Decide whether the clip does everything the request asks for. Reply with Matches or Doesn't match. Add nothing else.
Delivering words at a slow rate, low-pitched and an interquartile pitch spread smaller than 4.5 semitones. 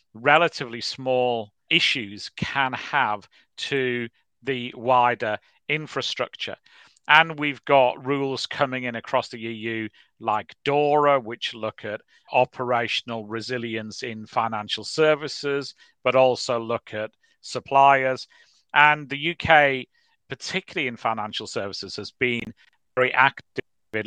Matches